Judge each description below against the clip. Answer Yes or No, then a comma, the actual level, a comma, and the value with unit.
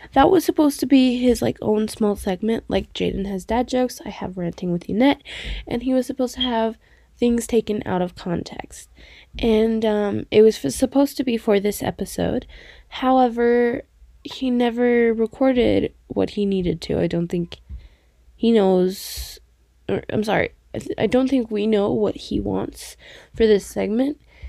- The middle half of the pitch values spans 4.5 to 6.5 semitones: No, average, 4.0 semitones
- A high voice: Yes, high, 225 Hz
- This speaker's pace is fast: No, average, 175 wpm